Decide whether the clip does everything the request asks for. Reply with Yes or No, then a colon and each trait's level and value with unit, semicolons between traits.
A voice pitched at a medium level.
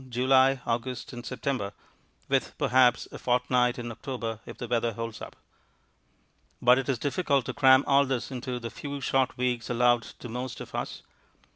No: low, 125 Hz